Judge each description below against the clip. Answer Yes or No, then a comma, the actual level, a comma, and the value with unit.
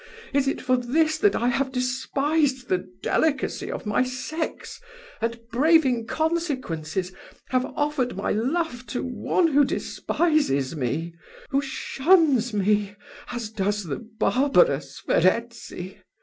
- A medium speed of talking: No, slow, 120 wpm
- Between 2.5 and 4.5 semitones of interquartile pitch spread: No, wide, 5.5 semitones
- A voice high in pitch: Yes, very high, 255 Hz